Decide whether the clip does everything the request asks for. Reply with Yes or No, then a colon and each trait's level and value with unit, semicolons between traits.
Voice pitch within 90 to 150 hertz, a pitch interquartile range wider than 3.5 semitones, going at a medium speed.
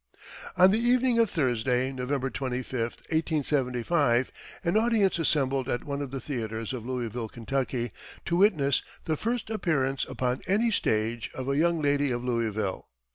Yes: low, 135 Hz; wide, 5.5 semitones; average, 150 wpm